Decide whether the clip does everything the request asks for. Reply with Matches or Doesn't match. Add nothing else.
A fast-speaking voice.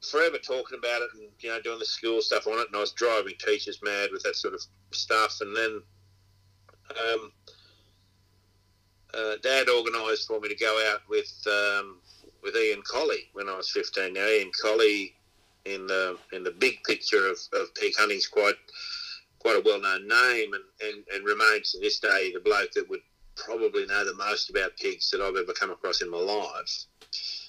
Doesn't match